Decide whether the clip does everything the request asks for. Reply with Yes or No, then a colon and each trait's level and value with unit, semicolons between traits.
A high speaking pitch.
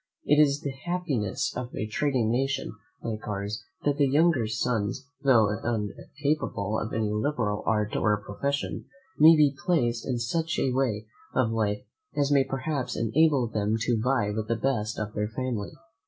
No: low, 120 Hz